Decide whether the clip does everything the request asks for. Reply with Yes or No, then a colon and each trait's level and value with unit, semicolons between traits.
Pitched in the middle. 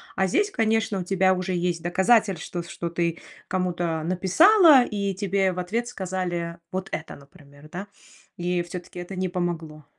Yes: medium, 180 Hz